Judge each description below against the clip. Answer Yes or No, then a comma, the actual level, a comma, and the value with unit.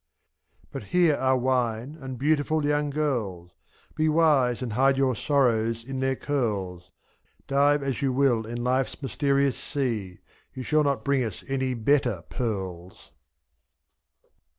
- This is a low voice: Yes, low, 130 Hz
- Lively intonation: No, average, 3.5 semitones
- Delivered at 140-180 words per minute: Yes, average, 145 wpm